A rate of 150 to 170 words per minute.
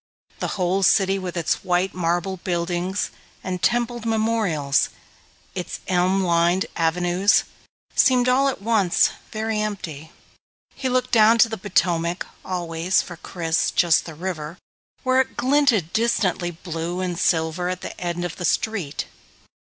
No: average, 140 wpm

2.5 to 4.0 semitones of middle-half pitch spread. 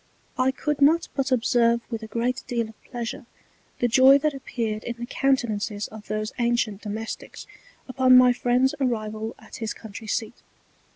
Yes: average, 2.8 semitones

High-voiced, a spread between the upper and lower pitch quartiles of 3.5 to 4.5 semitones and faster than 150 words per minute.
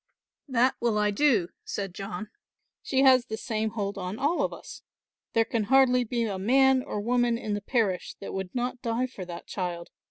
Yes: high, 225 Hz; average, 4.0 semitones; average, 195 wpm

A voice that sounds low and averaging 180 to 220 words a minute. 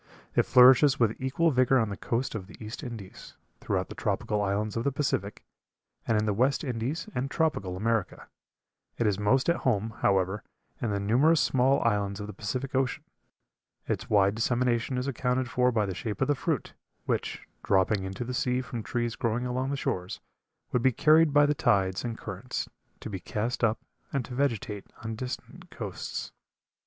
Yes: low, 120 Hz; average, 185 wpm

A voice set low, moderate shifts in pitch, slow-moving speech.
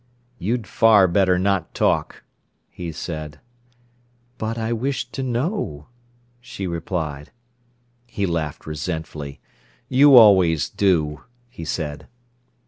No: very low, 90 Hz; wide, 6.4 semitones; slow, 105 wpm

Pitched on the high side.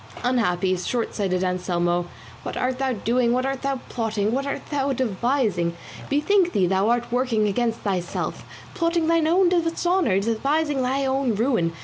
Yes: high, 245 Hz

